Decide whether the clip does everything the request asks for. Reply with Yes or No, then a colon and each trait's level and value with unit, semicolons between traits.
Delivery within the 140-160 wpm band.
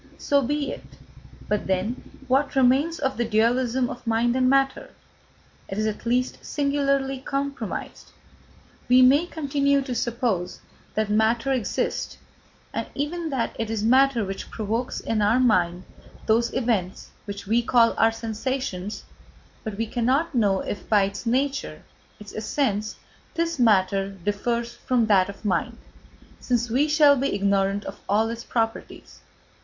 Yes: average, 145 wpm